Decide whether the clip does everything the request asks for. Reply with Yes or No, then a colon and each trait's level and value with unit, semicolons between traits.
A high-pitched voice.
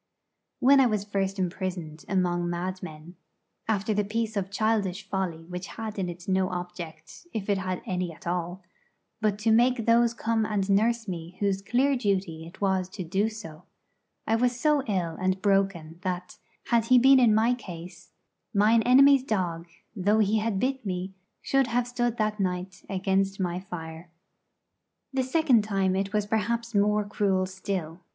Yes: high, 195 Hz